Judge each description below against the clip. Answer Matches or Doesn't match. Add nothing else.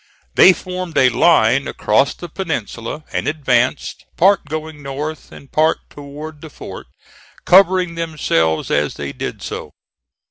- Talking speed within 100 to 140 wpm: Matches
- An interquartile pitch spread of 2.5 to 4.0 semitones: Doesn't match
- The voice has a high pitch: Doesn't match